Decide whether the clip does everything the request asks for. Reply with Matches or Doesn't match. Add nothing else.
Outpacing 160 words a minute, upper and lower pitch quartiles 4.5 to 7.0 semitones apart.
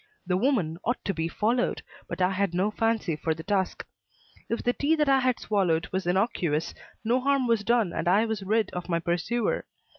Matches